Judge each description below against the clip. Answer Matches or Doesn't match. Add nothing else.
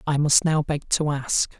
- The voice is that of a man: Matches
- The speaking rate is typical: Doesn't match